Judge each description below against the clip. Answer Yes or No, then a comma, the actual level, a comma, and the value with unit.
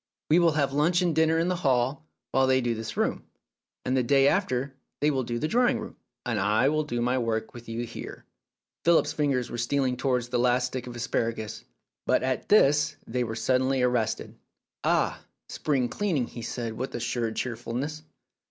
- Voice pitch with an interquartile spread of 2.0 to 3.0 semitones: No, average, 3.8 semitones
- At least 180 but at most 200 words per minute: Yes, average, 190 wpm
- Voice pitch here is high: No, low, 130 Hz